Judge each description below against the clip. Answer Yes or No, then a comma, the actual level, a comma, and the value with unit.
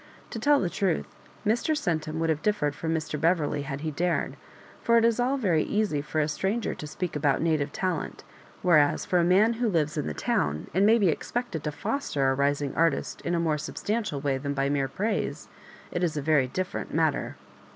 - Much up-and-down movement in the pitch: Yes, wide, 5.7 semitones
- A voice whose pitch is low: No, medium, 160 Hz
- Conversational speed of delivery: No, fast, 220 wpm